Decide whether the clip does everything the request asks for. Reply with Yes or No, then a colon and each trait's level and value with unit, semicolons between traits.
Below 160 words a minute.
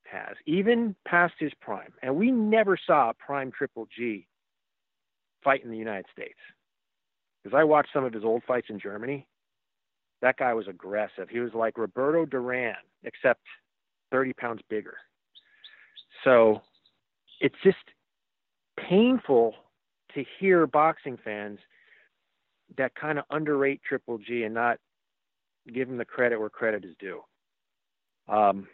Yes: average, 140 wpm